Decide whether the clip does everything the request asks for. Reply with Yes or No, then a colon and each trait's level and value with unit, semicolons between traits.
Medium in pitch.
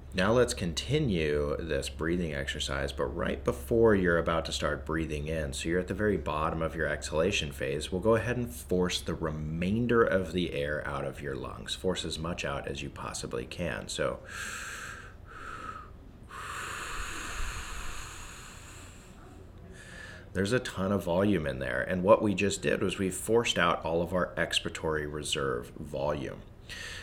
No: very low, 85 Hz